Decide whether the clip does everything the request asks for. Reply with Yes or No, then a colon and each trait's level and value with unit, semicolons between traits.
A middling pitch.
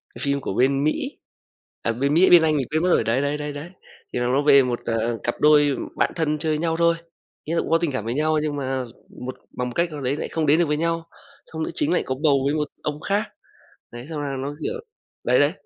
Yes: medium, 150 Hz